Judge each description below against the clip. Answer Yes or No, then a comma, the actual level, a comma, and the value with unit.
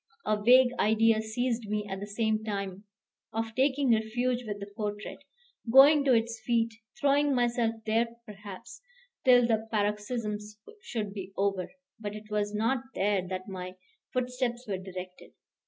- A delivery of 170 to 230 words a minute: No, average, 150 wpm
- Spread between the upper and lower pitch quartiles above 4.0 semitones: No, average, 2.9 semitones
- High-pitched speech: Yes, high, 220 Hz